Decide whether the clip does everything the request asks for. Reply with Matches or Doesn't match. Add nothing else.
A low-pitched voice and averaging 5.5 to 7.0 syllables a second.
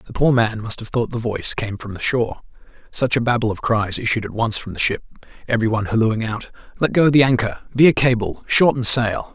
Matches